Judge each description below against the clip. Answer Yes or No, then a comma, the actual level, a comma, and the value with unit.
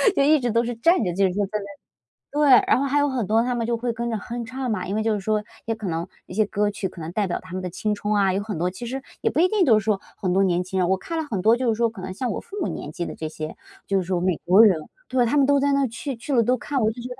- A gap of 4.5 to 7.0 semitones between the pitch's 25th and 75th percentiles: Yes, average, 4.8 semitones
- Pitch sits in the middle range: No, high, 220 Hz